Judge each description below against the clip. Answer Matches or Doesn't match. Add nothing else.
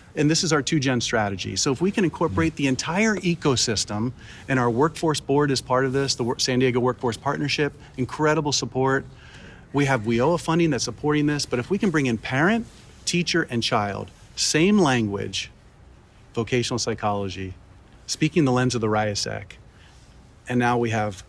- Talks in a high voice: Doesn't match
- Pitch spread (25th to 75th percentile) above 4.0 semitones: Matches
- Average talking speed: Matches